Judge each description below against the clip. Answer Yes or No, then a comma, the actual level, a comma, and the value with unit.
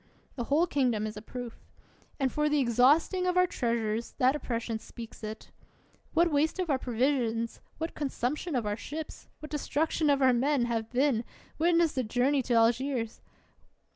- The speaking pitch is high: Yes, very high, 260 Hz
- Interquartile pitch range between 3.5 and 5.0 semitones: Yes, average, 4.4 semitones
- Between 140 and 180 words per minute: Yes, average, 170 wpm